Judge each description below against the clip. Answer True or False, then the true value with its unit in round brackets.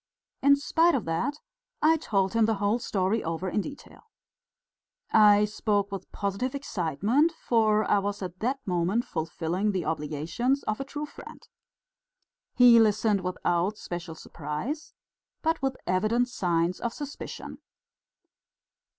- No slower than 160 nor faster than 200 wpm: False (135 wpm)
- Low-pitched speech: False (210 Hz)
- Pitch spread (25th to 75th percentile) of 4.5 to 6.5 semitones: True (5.3 semitones)